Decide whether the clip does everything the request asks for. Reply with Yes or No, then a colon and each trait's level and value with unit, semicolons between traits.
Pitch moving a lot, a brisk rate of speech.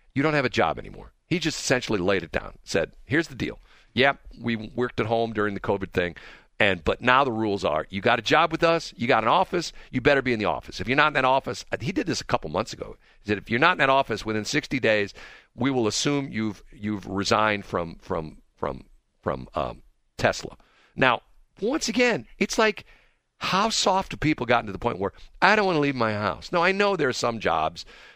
Yes: wide, 6.3 semitones; fast, 240 wpm